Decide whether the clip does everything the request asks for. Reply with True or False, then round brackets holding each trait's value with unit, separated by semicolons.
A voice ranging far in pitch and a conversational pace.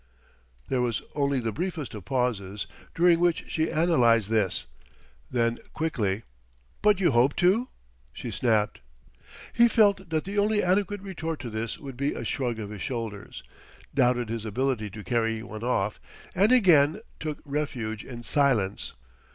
True (6.8 semitones; 150 wpm)